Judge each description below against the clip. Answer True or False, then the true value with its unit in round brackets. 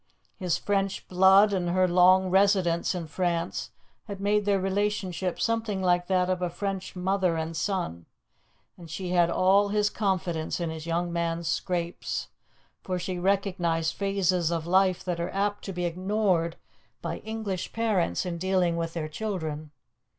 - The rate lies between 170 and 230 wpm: False (160 wpm)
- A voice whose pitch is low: False (185 Hz)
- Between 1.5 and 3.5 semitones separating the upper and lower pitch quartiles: True (2.4 semitones)